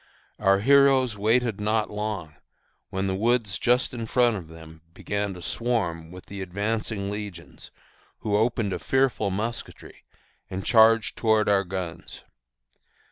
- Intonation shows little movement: No, average, 3.3 semitones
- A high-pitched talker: No, low, 105 Hz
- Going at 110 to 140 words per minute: Yes, slow, 135 wpm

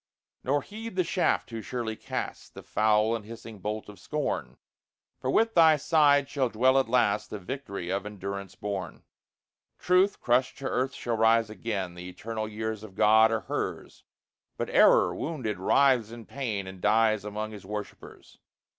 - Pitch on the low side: Yes, low, 110 Hz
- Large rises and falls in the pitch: No, average, 4.1 semitones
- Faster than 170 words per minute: No, average, 165 wpm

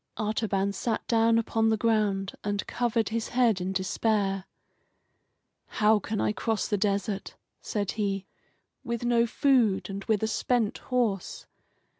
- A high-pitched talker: Yes, high, 215 Hz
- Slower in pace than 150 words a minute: Yes, average, 140 wpm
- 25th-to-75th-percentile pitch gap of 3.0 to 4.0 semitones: No, narrow, 2.5 semitones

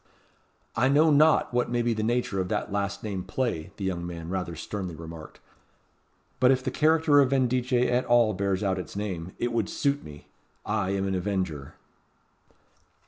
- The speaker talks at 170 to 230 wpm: Yes, average, 185 wpm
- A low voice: Yes, low, 105 Hz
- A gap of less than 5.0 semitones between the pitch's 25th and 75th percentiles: No, average, 5.3 semitones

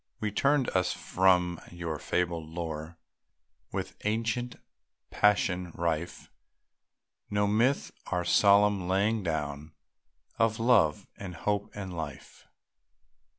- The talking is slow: Yes, slow, 105 wpm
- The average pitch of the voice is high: No, very low, 95 Hz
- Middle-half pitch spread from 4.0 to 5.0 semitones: No, average, 3.6 semitones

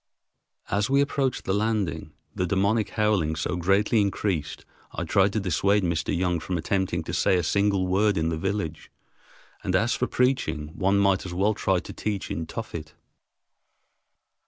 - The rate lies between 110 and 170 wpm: Yes, average, 165 wpm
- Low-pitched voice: Yes, very low, 95 Hz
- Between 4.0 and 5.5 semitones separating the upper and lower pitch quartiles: No, average, 3.2 semitones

